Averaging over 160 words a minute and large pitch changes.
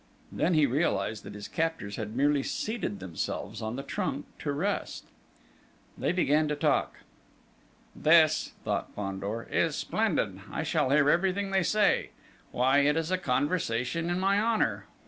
No: average, 150 wpm; wide, 6.9 semitones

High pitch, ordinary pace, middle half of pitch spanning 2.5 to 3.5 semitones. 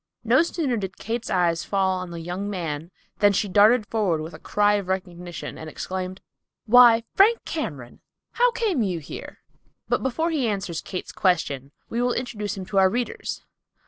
No: high, 200 Hz; average, 175 wpm; average, 5.1 semitones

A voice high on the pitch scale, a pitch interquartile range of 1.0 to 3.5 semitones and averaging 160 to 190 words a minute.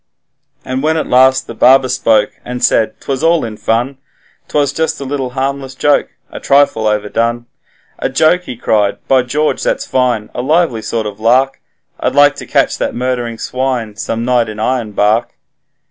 No: low, 125 Hz; average, 3.1 semitones; average, 175 wpm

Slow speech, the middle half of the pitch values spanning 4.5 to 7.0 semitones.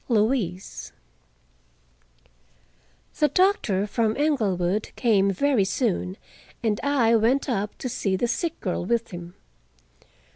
Yes: slow, 110 wpm; average, 5.1 semitones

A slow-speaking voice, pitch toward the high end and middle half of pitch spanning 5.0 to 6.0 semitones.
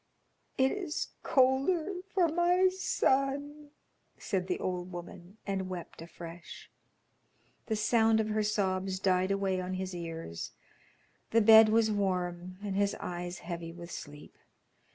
Yes: slow, 130 wpm; high, 195 Hz; average, 5.3 semitones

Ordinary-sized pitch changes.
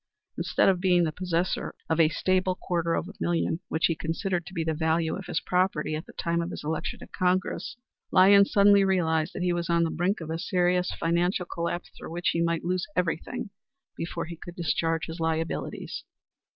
No: narrow, 1.9 semitones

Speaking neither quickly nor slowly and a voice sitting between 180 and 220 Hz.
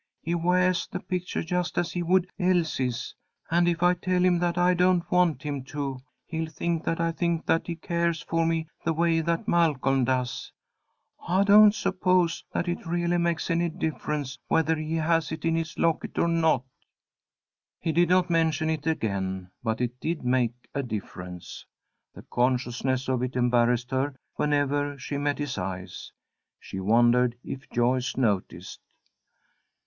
No: average, 165 wpm; medium, 160 Hz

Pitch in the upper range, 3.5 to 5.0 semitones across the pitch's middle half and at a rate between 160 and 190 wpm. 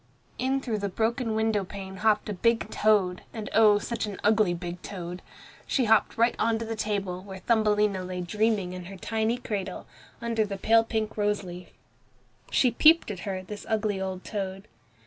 No: high, 210 Hz; average, 2.8 semitones; average, 180 wpm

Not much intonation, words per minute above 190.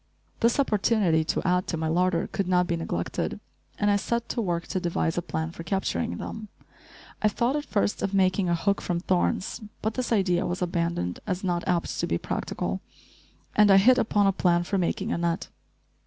No: average, 3.2 semitones; average, 200 wpm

